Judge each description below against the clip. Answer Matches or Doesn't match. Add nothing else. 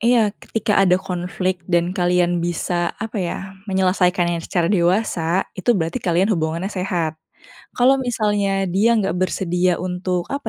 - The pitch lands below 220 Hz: Matches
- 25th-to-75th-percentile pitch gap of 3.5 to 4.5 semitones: Doesn't match